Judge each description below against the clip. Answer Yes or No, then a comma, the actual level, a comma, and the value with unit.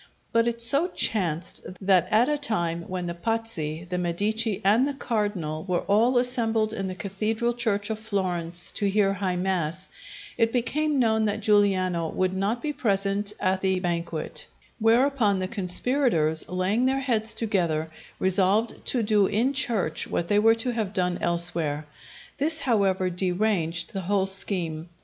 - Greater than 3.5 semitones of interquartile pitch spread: Yes, average, 4.1 semitones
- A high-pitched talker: Yes, high, 200 Hz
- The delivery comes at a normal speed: Yes, average, 160 wpm